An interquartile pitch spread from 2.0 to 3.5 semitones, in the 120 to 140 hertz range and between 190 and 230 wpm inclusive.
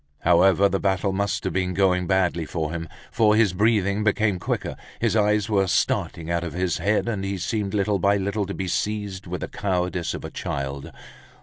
No: narrow, 2.4 semitones; very low, 95 Hz; average, 200 wpm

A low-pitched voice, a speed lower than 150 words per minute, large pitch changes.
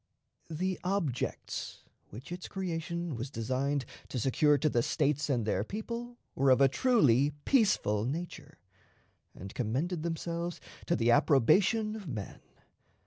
No: medium, 150 Hz; slow, 135 wpm; wide, 5.7 semitones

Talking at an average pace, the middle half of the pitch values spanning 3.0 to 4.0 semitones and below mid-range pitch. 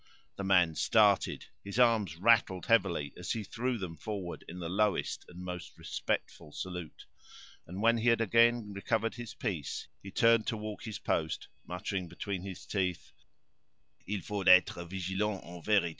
Yes: average, 160 wpm; average, 3.6 semitones; low, 100 Hz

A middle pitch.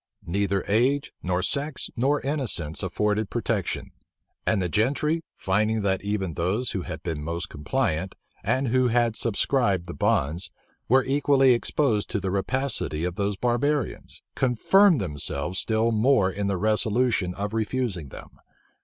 No: low, 105 Hz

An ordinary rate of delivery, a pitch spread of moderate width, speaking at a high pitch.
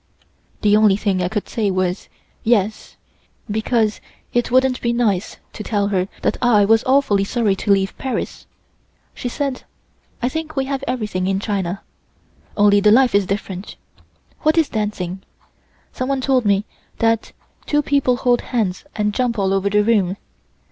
Yes: average, 160 wpm; average, 4.1 semitones; high, 215 Hz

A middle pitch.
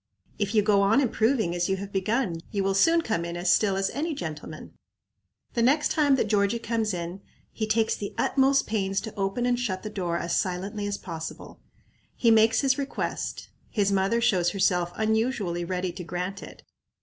No: high, 200 Hz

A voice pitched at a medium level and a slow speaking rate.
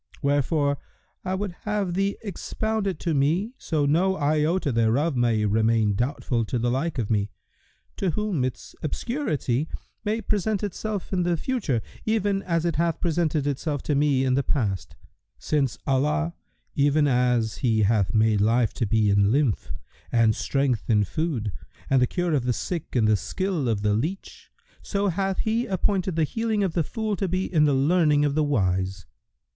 No: medium, 145 Hz; average, 175 wpm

